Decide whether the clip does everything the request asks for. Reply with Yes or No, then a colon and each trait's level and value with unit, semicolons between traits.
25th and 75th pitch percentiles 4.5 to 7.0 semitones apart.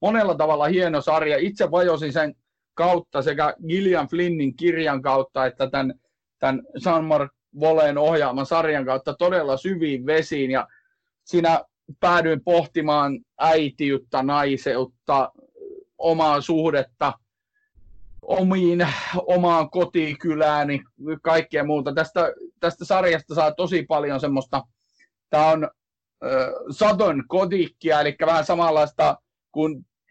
No: average, 3.3 semitones